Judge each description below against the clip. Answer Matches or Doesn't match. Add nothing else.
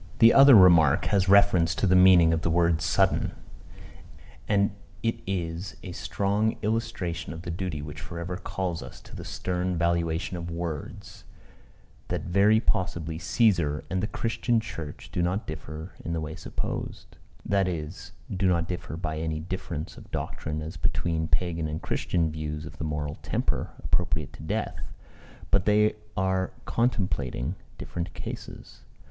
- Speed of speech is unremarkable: Matches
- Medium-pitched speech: Doesn't match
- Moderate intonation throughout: Matches